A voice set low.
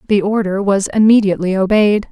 No: high, 200 Hz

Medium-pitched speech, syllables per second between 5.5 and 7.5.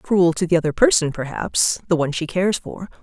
Yes: medium, 175 Hz; 5.8 syllables/s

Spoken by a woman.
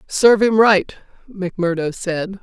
Yes: female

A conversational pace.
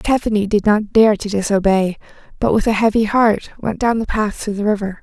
No: fast, 215 wpm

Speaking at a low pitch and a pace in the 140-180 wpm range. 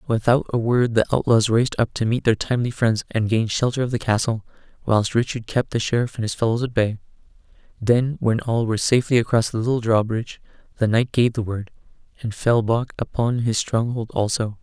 No: low, 115 Hz; fast, 205 wpm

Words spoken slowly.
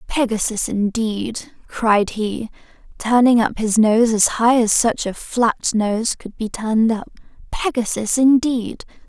Yes: slow, 130 wpm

